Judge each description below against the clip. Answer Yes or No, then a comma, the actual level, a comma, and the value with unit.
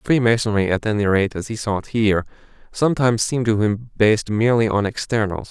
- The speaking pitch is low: Yes, low, 110 Hz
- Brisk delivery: No, average, 185 wpm